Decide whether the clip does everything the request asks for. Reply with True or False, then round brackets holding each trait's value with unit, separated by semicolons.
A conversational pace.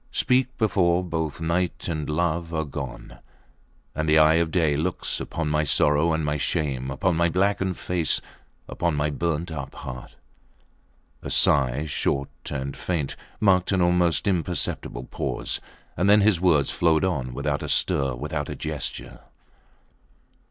True (150 wpm)